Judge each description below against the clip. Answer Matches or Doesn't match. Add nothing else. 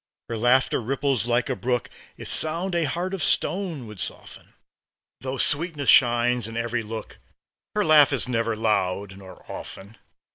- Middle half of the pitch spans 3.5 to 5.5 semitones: Matches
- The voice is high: Doesn't match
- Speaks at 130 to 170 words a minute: Matches